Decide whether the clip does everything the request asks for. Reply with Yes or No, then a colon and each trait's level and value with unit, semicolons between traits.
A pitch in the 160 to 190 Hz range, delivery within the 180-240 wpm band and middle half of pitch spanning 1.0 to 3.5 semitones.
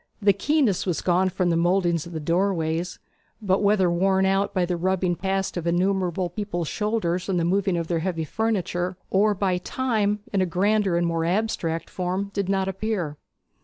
Yes: medium, 185 Hz; average, 185 wpm; narrow, 2.5 semitones